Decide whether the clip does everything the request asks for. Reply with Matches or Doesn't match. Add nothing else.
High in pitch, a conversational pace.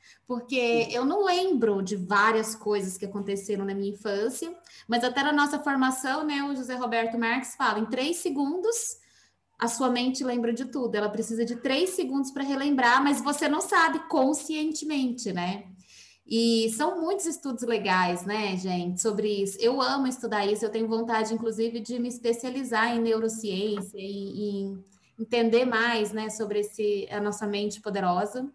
Matches